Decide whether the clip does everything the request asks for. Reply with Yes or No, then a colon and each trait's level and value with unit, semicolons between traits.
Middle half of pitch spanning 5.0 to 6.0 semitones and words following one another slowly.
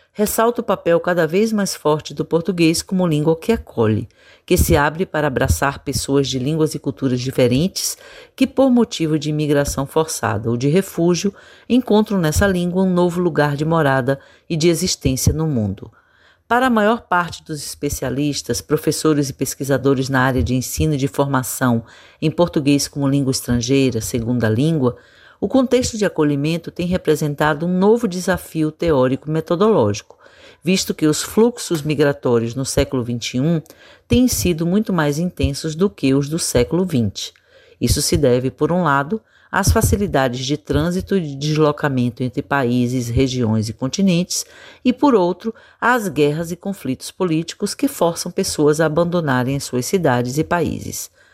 No: average, 5.3 semitones; average, 160 wpm